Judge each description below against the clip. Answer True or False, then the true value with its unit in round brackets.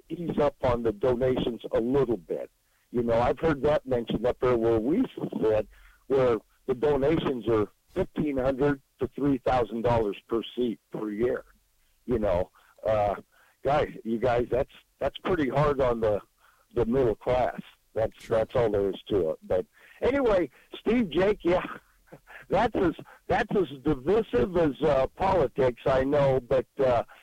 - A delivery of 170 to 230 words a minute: False (160 wpm)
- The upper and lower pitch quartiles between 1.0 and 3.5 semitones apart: False (5.0 semitones)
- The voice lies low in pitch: True (130 Hz)